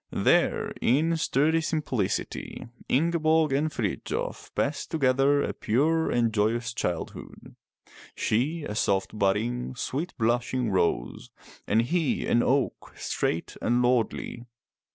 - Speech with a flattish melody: No, average, 5.3 semitones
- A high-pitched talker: No, low, 125 Hz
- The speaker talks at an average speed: No, slow, 115 wpm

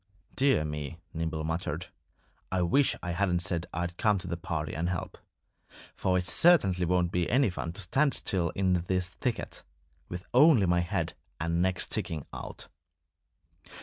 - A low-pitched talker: Yes, very low, 90 Hz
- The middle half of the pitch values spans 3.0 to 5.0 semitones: No, narrow, 2.4 semitones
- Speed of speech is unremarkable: Yes, average, 160 wpm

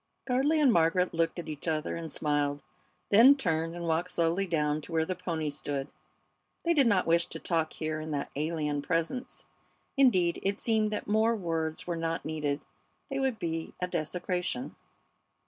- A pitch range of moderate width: Yes, average, 3.9 semitones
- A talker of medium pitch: Yes, medium, 165 Hz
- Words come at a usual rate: Yes, average, 175 wpm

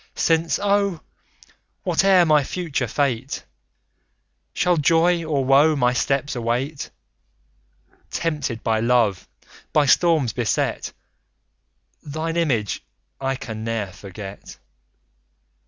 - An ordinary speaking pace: No, slow, 95 wpm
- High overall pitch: No, medium, 140 Hz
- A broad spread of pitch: Yes, wide, 5.7 semitones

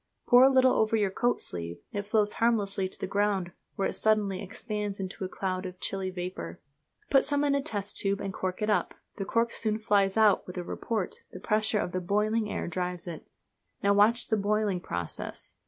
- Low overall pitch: No, high, 200 Hz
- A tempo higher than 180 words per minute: Yes, fast, 205 wpm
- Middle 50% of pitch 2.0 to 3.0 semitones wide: Yes, average, 2.7 semitones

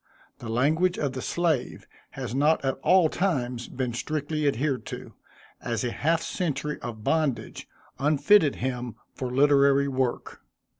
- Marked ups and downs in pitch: No, average, 3.6 semitones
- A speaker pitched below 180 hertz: Yes, medium, 140 Hz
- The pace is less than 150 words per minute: Yes, average, 140 wpm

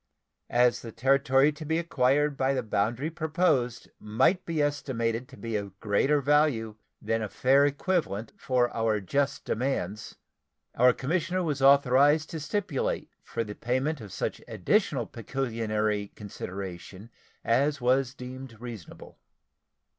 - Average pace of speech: No, slow, 130 wpm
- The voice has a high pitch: No, low, 130 Hz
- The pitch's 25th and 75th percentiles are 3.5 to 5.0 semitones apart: Yes, average, 4.5 semitones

